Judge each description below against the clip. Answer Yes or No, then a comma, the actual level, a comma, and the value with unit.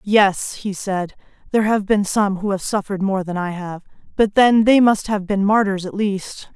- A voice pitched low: No, high, 200 Hz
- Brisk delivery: Yes, fast, 210 wpm